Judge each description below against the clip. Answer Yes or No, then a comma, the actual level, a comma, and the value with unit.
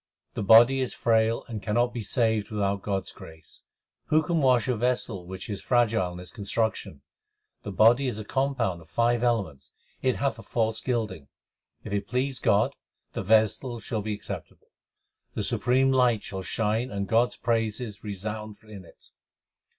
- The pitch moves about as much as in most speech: Yes, average, 3.3 semitones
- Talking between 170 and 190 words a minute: Yes, average, 175 wpm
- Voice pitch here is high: No, low, 110 Hz